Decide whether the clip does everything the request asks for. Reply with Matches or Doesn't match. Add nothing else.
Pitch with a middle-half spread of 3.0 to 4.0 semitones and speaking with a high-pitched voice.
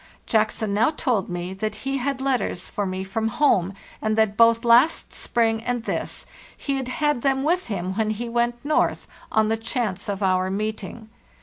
Matches